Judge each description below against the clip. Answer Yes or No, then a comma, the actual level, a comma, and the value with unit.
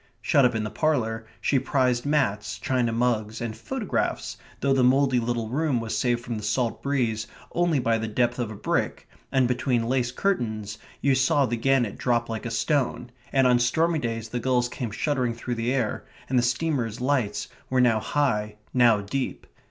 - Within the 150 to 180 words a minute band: No, average, 190 wpm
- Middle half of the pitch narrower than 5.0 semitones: Yes, average, 2.8 semitones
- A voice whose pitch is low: Yes, low, 125 Hz